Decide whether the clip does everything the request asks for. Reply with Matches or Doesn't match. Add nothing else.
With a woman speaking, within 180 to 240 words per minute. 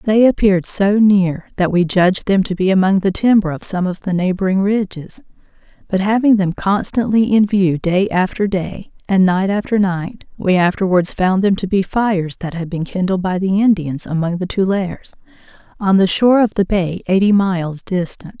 Matches